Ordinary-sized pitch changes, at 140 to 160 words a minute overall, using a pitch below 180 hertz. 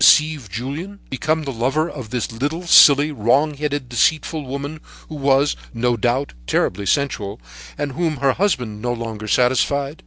Yes: average, 3.8 semitones; average, 155 wpm; medium, 140 Hz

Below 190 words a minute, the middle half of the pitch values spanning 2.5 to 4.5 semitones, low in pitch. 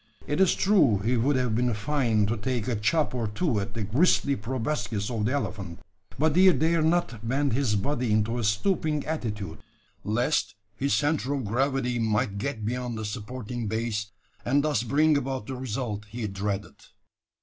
No: average, 175 wpm; average, 4.9 semitones; low, 120 Hz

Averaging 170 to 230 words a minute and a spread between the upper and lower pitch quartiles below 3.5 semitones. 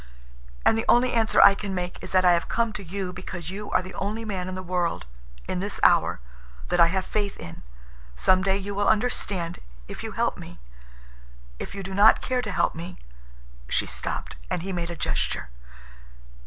Yes: average, 195 wpm; average, 2.9 semitones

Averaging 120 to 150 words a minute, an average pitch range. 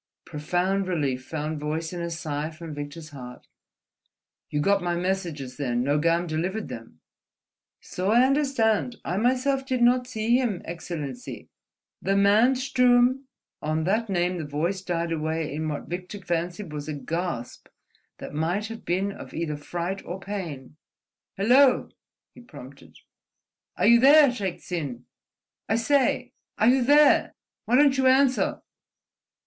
No: average, 145 wpm; wide, 7.2 semitones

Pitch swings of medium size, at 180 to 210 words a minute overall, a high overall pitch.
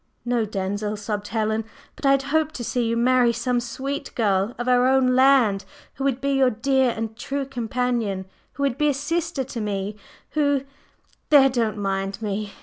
Yes: average, 4.1 semitones; average, 185 wpm; high, 245 Hz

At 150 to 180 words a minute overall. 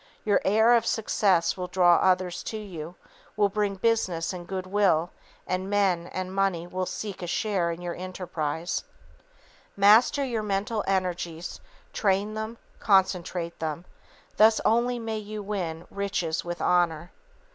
No: average, 140 wpm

